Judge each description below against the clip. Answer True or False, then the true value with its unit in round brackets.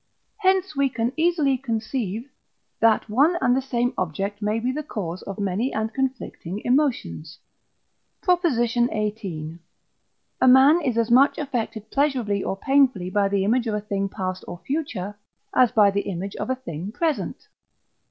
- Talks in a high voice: True (230 Hz)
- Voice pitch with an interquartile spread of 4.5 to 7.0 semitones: True (5.1 semitones)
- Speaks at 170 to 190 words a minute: False (160 wpm)